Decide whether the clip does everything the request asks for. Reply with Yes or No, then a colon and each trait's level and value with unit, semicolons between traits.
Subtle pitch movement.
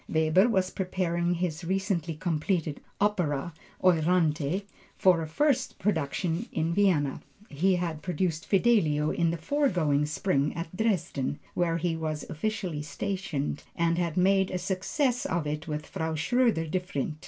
No: average, 3.4 semitones